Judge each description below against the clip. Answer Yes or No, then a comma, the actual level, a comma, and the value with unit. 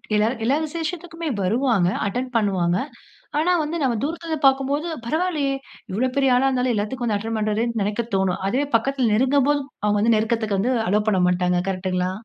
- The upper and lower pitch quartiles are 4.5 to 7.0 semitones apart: Yes, average, 5.1 semitones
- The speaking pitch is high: Yes, high, 235 Hz